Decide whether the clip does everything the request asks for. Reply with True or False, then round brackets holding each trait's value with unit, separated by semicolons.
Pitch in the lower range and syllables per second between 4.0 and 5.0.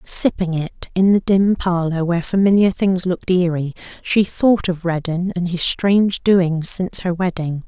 False (180 Hz; 4.5 syllables/s)